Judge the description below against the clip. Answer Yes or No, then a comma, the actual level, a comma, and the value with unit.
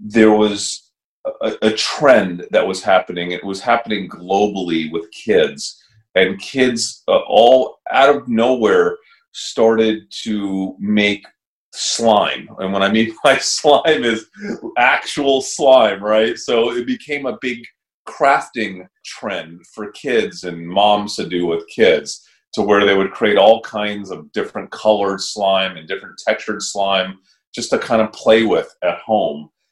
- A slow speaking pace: No, average, 145 wpm